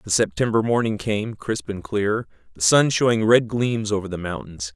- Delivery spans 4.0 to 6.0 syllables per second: Yes, 4.7 syllables/s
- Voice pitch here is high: No, low, 105 Hz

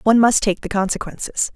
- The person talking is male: No, female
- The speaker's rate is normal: Yes, average, 195 wpm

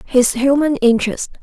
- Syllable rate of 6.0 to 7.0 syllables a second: No, 4.9 syllables/s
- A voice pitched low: No, very high, 260 Hz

